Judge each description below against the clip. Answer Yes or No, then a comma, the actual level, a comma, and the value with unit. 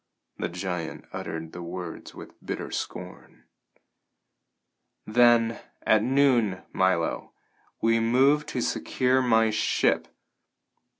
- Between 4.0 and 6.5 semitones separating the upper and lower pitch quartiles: Yes, average, 5.2 semitones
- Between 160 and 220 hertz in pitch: No, low, 115 Hz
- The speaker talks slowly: Yes, slow, 100 wpm